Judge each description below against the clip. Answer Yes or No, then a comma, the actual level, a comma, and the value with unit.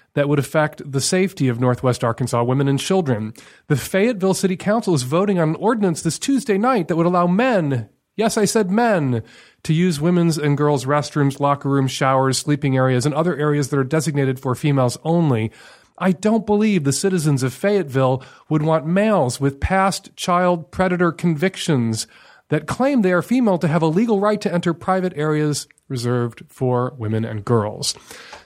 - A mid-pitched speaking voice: Yes, medium, 155 Hz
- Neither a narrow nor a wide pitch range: No, wide, 5.8 semitones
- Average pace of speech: Yes, average, 180 wpm